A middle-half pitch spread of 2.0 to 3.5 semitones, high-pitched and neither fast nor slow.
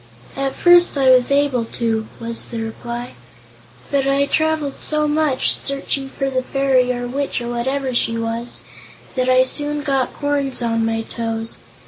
Yes: average, 2.9 semitones; very high, 260 Hz; average, 160 wpm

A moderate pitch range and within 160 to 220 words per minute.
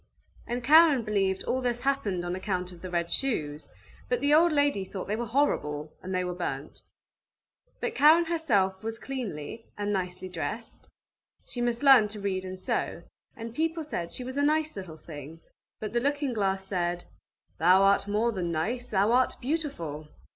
No: wide, 6.2 semitones; average, 180 wpm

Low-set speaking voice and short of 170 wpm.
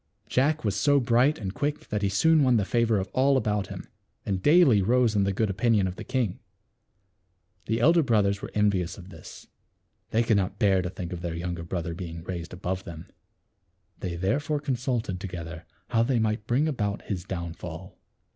No: low, 105 Hz; average, 195 wpm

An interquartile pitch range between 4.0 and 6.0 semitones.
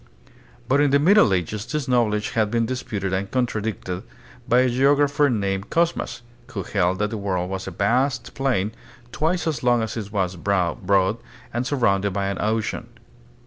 Yes: average, 4.7 semitones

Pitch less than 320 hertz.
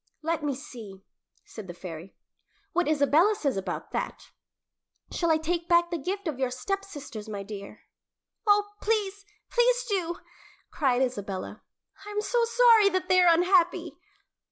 No: very high, 335 Hz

